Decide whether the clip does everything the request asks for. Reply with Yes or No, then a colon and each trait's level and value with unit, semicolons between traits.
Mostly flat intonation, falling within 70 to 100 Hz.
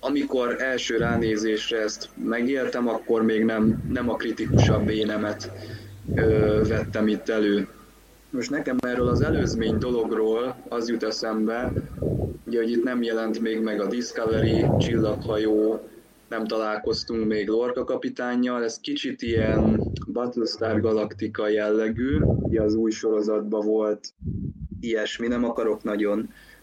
No: narrow, 1.4 semitones; low, 110 Hz